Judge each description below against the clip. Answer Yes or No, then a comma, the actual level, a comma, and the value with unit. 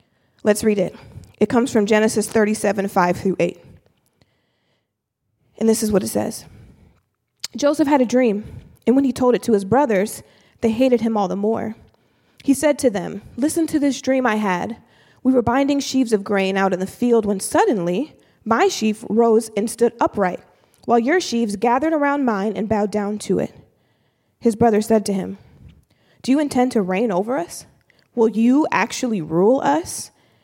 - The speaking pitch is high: Yes, high, 225 Hz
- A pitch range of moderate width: Yes, average, 4.0 semitones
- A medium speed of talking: Yes, average, 180 wpm